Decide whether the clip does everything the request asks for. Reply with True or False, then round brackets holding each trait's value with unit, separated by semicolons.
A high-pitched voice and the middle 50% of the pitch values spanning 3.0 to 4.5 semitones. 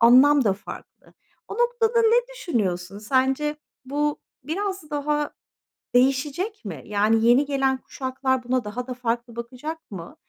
True (260 Hz; 4.1 semitones)